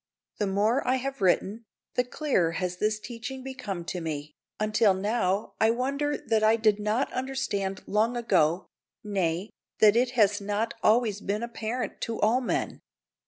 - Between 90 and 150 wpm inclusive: No, average, 160 wpm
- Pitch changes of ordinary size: Yes, average, 3.7 semitones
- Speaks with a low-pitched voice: No, high, 215 Hz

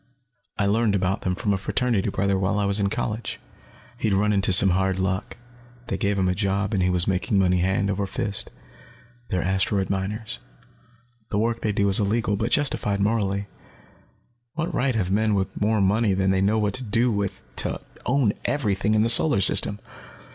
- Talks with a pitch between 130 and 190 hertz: No, low, 100 Hz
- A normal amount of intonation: No, narrow, 2.2 semitones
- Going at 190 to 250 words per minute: Yes, average, 200 wpm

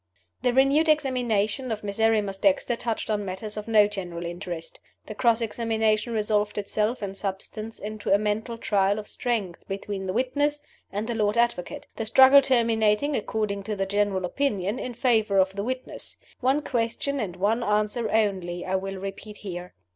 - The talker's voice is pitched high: Yes, high, 215 Hz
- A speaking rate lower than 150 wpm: No, average, 170 wpm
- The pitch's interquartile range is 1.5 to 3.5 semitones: Yes, average, 3.0 semitones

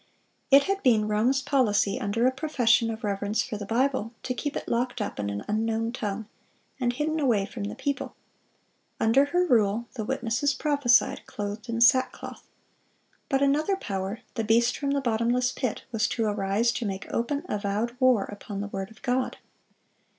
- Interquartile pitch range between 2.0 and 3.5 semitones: No, average, 3.9 semitones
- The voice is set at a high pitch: Yes, high, 235 Hz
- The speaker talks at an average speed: Yes, average, 170 wpm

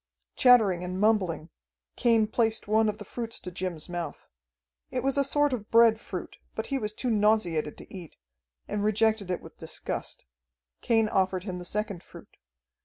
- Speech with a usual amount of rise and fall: Yes, average, 3.6 semitones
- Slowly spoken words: No, average, 175 wpm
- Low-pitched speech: No, high, 210 Hz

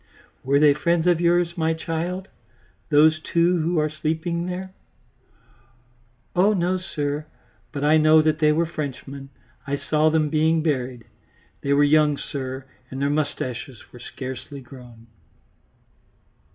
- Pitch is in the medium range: Yes, medium, 155 Hz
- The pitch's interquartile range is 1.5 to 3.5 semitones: Yes, average, 3.0 semitones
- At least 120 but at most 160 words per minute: Yes, average, 140 wpm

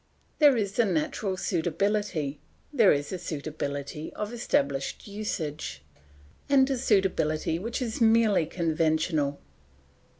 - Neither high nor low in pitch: Yes, medium, 180 Hz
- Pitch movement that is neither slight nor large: No, wide, 5.8 semitones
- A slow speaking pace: Yes, slow, 110 wpm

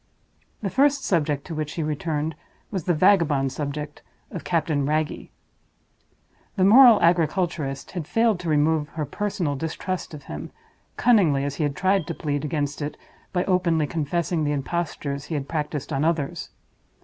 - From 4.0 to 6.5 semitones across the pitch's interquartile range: No, average, 3.5 semitones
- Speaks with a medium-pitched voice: Yes, medium, 155 Hz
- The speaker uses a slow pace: No, average, 160 wpm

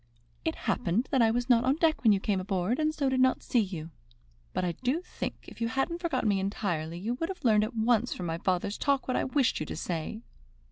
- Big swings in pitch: Yes, wide, 5.7 semitones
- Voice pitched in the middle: No, high, 230 Hz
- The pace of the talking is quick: Yes, fast, 245 wpm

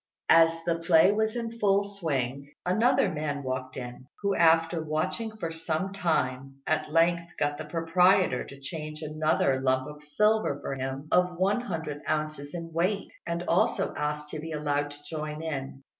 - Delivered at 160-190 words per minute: Yes, average, 165 wpm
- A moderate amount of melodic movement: Yes, average, 3.5 semitones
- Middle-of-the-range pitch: Yes, medium, 160 Hz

